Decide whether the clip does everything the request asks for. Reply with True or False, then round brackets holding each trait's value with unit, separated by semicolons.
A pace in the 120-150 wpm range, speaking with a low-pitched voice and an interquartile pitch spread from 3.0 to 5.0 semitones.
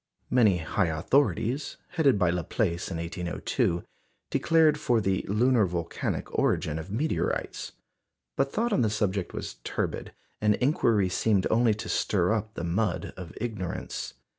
False (140 wpm; 105 Hz; 5.5 semitones)